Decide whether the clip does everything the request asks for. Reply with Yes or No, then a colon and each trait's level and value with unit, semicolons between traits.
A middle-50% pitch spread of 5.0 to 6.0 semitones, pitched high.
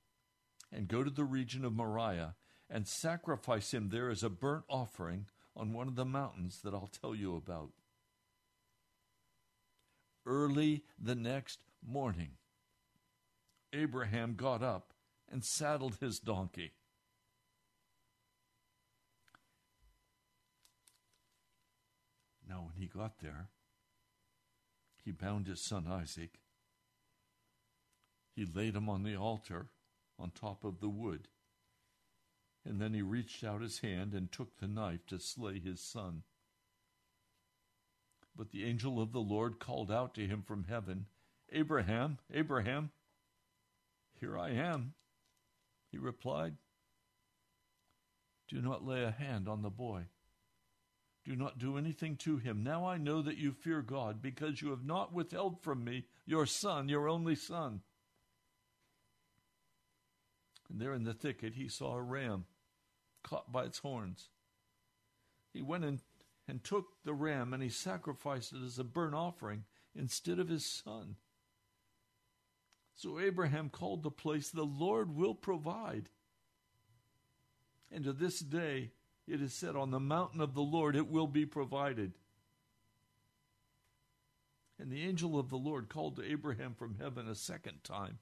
No: wide, 5.4 semitones; low, 115 Hz